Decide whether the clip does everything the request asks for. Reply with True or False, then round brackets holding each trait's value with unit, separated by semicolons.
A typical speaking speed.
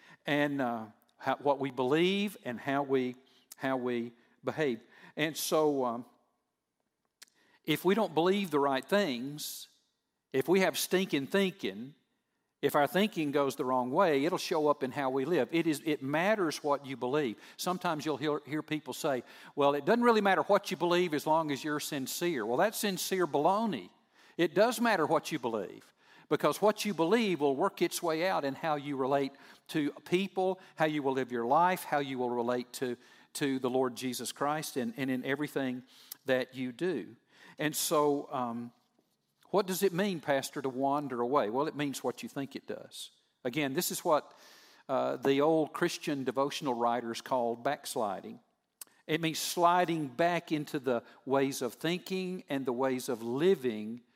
True (175 wpm)